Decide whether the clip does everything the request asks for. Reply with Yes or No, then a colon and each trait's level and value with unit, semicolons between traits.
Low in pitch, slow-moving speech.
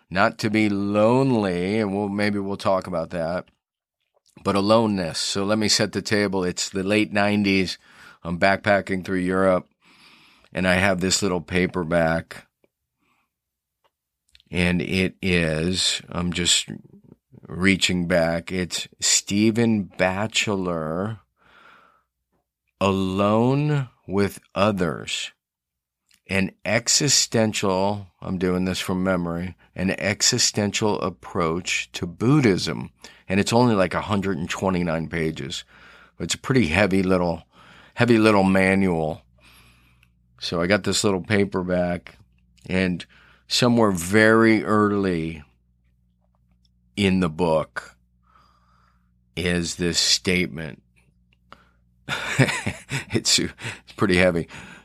Yes: very low, 95 Hz; slow, 100 wpm